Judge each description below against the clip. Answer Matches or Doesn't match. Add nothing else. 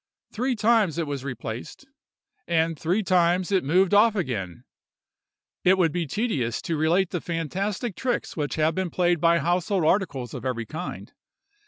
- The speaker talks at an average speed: Matches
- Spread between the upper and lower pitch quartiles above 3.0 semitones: Matches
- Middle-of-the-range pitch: Matches